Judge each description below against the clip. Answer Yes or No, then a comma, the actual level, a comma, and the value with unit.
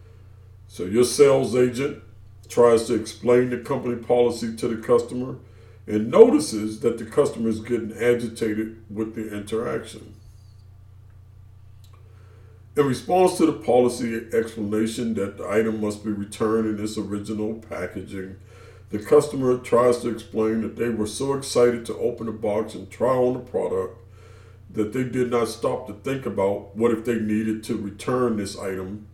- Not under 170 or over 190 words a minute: No, average, 155 wpm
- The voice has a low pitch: Yes, low, 110 Hz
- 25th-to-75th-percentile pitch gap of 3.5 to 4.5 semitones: No, average, 3.0 semitones